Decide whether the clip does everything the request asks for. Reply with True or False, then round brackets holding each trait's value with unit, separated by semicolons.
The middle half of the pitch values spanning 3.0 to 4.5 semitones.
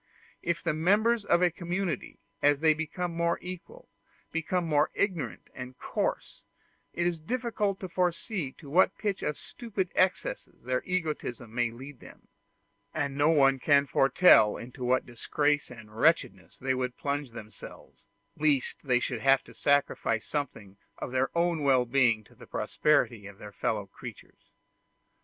False (5.4 semitones)